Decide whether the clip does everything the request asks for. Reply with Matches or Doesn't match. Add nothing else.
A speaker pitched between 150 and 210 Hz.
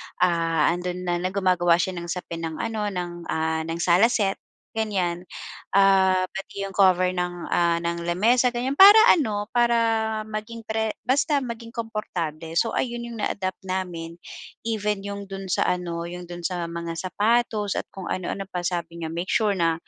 Matches